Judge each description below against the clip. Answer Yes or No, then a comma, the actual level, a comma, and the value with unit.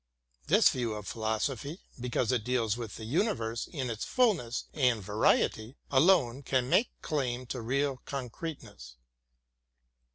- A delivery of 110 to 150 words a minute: Yes, slow, 135 wpm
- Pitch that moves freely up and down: No, average, 3.8 semitones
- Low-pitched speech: Yes, low, 125 Hz